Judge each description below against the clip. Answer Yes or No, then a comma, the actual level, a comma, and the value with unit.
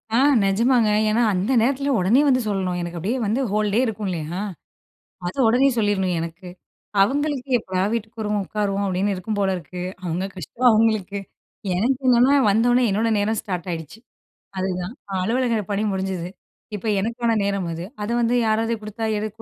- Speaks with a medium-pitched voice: No, high, 210 Hz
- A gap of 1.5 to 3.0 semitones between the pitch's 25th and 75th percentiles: No, average, 3.7 semitones